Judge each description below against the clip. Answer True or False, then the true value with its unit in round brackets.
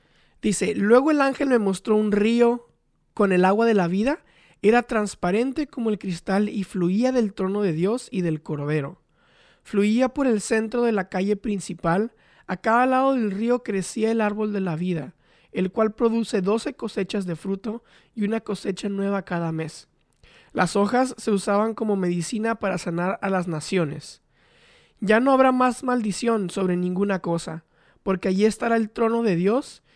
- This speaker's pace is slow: False (170 wpm)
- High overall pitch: True (210 Hz)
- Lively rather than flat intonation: False (3.6 semitones)